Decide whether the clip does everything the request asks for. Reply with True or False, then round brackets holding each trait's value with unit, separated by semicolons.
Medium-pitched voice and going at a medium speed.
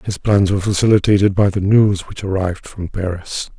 False (100 Hz; 185 wpm)